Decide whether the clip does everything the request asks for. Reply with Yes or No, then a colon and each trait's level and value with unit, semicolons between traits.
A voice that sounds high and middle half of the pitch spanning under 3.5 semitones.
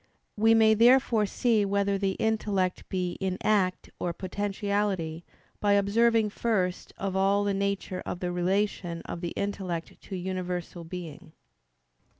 Yes: high, 195 Hz; narrow, 2.4 semitones